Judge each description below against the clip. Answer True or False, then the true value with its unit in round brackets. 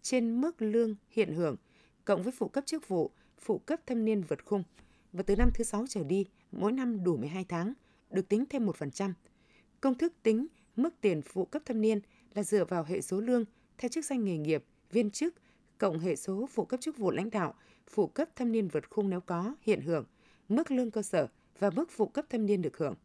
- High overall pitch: True (215 Hz)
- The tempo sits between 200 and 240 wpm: True (225 wpm)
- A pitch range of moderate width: True (4.4 semitones)